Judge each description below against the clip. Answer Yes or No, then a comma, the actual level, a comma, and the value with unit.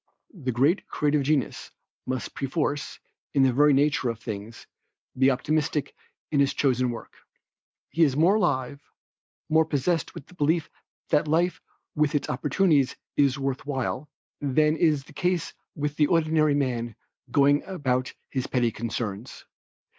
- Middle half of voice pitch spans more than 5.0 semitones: No, average, 3.2 semitones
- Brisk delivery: No, average, 145 wpm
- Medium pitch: Yes, medium, 145 Hz